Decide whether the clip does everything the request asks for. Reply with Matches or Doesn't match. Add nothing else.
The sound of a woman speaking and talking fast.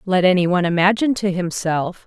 Doesn't match